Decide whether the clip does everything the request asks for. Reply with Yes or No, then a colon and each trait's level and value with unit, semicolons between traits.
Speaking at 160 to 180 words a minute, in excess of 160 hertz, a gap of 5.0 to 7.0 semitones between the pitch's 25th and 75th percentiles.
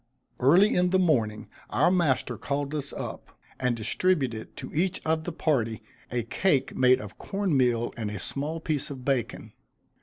No: average, 170 wpm; medium, 140 Hz; wide, 5.4 semitones